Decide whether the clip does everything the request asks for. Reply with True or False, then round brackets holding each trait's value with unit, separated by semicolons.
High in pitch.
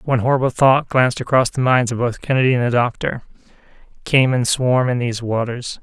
False (125 Hz)